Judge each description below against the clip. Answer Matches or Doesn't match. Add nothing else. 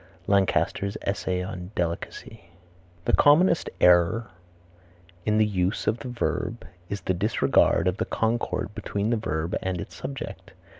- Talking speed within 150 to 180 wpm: Doesn't match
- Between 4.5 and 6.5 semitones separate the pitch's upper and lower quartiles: Doesn't match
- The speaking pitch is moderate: Doesn't match